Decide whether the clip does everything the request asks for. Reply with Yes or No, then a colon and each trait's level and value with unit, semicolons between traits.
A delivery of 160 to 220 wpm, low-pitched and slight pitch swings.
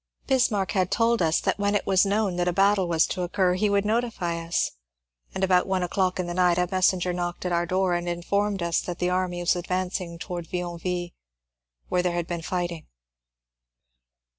No: average, 200 wpm; medium, 180 Hz; narrow, 1.7 semitones